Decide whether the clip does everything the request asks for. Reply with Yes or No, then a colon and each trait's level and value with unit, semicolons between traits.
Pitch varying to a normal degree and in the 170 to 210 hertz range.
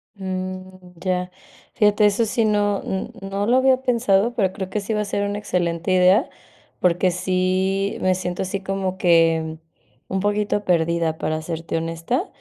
No: narrow, 2.3 semitones; high, 190 Hz